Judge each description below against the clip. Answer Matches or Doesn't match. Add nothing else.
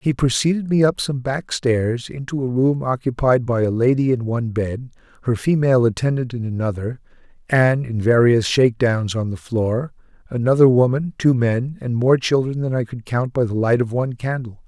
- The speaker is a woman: Doesn't match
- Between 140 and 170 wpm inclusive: Doesn't match